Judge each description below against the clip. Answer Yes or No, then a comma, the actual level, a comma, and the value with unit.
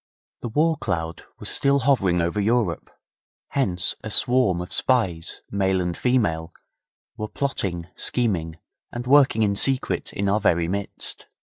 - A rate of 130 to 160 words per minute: Yes, average, 140 wpm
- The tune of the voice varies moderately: No, wide, 6.4 semitones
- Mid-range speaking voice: No, low, 100 Hz